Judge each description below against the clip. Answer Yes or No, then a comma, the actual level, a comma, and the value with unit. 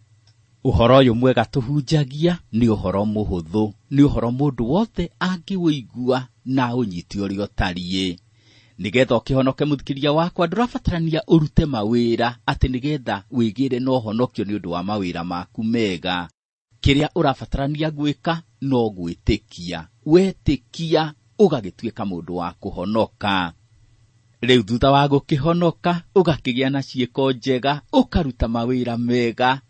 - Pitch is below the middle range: Yes, low, 125 Hz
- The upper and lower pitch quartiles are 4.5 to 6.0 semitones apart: Yes, average, 5.0 semitones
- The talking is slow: Yes, slow, 115 wpm